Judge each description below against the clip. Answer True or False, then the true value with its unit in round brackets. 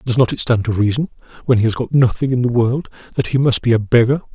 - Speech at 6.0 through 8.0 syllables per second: True (6.5 syllables/s)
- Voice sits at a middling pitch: False (120 Hz)